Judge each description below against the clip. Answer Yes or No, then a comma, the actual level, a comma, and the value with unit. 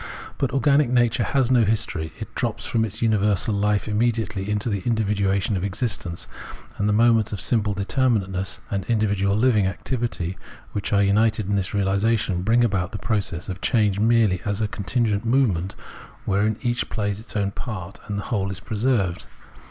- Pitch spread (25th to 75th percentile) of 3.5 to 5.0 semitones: No, average, 2.8 semitones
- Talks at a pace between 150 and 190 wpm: Yes, average, 170 wpm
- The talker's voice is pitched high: No, low, 105 Hz